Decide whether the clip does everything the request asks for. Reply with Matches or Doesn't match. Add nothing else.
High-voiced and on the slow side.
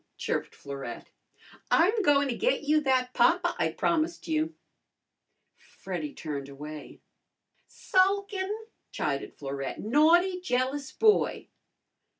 Matches